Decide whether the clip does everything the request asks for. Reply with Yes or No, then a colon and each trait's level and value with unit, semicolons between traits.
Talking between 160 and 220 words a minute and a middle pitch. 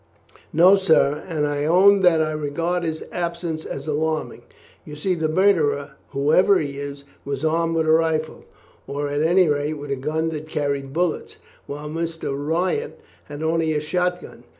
Yes: average, 175 wpm; medium, 155 Hz